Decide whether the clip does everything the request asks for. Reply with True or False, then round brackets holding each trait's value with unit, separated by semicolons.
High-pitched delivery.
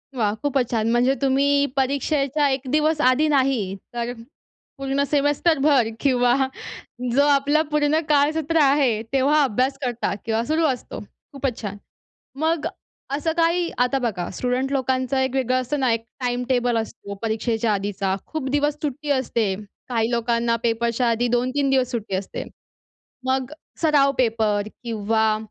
True (260 Hz)